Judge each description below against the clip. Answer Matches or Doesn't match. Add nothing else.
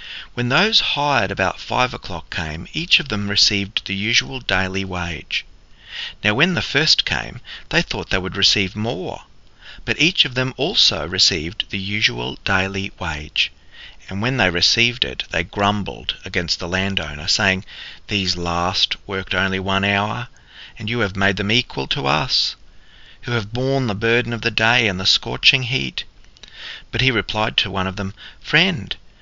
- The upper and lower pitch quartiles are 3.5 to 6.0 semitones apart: Matches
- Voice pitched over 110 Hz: Doesn't match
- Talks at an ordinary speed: Matches